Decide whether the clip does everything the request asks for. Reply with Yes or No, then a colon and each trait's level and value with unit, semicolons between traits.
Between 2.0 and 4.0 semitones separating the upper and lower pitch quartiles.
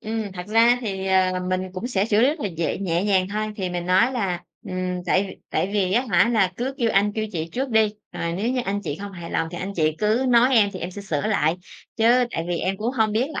Yes: average, 3.6 semitones